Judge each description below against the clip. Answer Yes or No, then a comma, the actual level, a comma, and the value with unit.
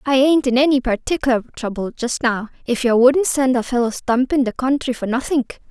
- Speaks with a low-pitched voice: No, very high, 255 Hz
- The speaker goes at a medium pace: Yes, average, 190 wpm